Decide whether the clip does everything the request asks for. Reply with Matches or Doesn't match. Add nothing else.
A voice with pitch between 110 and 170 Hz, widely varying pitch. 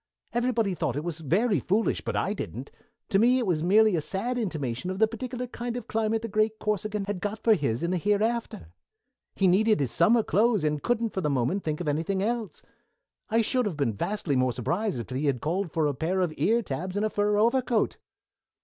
Doesn't match